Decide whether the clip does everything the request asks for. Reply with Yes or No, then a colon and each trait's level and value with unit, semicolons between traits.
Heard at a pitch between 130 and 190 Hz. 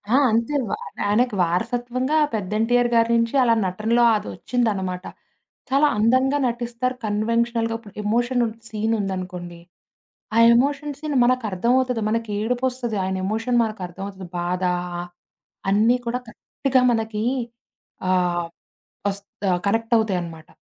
No: high, 225 Hz